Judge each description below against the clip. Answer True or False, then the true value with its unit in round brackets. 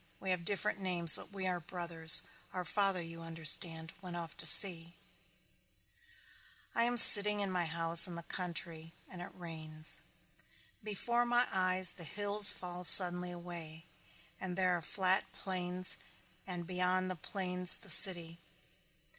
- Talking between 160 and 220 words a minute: False (150 wpm)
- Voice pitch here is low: False (180 Hz)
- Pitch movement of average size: False (2.1 semitones)